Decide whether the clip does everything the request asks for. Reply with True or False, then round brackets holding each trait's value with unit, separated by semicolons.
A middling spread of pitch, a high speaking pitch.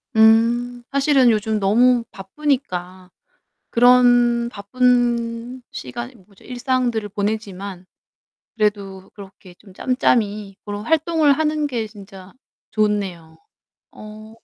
True (3.6 semitones; 220 Hz)